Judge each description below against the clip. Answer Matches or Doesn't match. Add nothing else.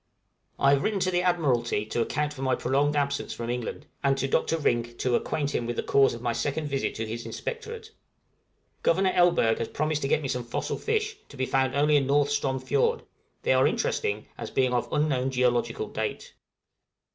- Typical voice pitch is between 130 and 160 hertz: Matches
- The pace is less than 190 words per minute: Doesn't match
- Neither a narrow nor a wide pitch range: Matches